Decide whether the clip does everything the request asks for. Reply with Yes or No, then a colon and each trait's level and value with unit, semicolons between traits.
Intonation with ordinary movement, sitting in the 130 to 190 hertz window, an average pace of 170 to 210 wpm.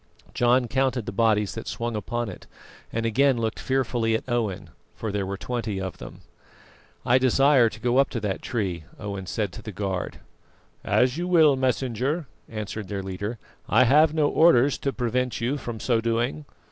No: average, 3.8 semitones; low, 115 Hz; average, 180 wpm